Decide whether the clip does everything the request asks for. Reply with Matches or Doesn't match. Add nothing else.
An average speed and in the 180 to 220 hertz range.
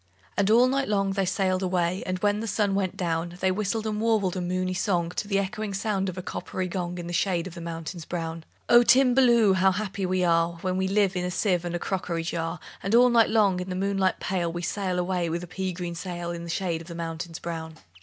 Doesn't match